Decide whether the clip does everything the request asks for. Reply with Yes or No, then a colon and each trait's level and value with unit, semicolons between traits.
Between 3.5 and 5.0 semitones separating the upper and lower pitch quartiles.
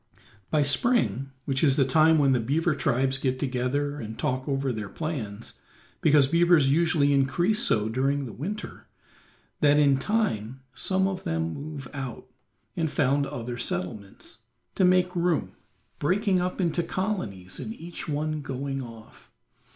Yes: average, 4.7 semitones